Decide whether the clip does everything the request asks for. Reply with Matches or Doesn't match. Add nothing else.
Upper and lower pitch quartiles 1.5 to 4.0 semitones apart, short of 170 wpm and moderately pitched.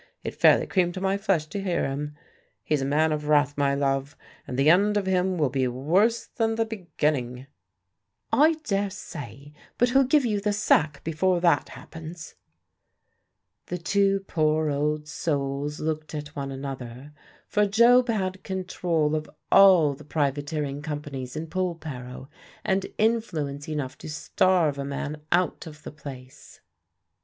Doesn't match